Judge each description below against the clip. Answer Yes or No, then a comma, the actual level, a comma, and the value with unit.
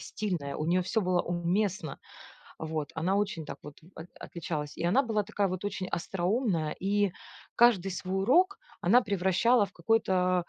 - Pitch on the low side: No, medium, 185 Hz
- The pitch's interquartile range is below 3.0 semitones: No, average, 3.3 semitones